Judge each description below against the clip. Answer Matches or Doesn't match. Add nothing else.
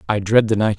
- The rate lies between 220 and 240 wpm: Doesn't match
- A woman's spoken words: Doesn't match